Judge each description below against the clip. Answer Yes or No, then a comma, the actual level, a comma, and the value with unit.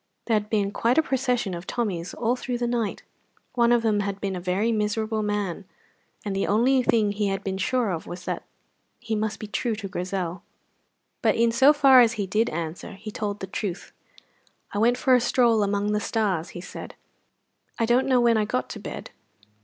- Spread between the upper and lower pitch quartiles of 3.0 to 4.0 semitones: Yes, average, 3.3 semitones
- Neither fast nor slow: No, fast, 210 wpm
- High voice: Yes, high, 215 Hz